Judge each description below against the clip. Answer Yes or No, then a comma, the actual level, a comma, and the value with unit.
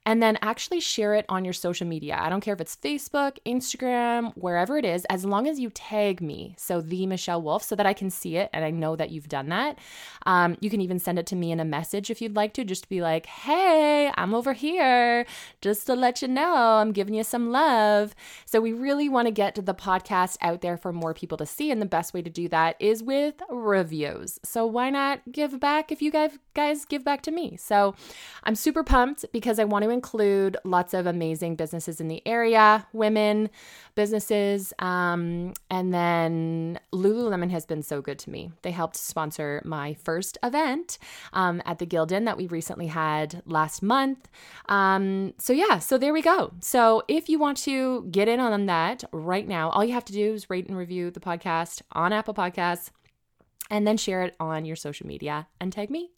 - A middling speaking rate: No, fast, 215 wpm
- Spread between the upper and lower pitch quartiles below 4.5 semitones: No, wide, 5.6 semitones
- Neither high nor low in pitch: No, high, 200 Hz